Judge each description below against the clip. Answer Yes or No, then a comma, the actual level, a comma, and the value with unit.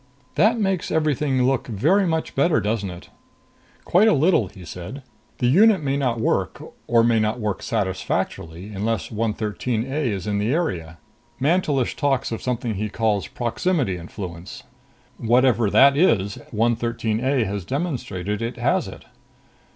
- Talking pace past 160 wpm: No, average, 150 wpm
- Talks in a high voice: No, low, 115 Hz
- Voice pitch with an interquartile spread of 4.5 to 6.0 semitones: Yes, wide, 5.4 semitones